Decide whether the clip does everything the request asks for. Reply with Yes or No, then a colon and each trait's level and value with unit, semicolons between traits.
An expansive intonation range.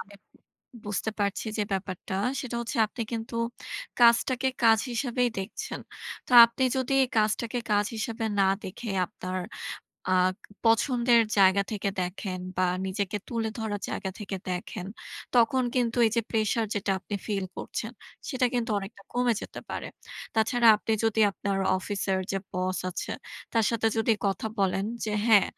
No: average, 3.1 semitones